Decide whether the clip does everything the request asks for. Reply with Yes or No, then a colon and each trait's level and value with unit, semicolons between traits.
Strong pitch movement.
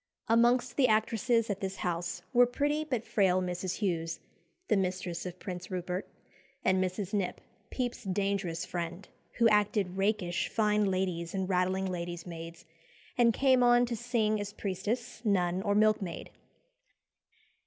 No: average, 3.7 semitones